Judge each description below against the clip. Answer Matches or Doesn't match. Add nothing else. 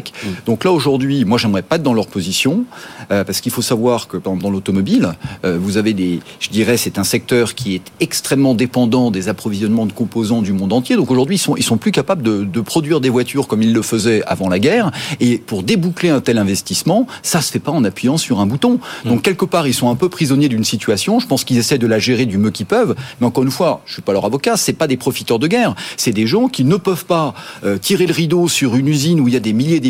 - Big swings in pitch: Matches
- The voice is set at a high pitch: Doesn't match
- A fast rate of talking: Matches